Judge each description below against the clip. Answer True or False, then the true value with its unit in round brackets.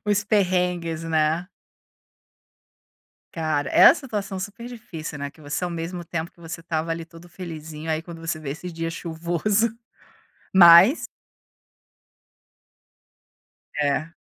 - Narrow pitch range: True (2.3 semitones)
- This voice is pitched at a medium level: True (165 Hz)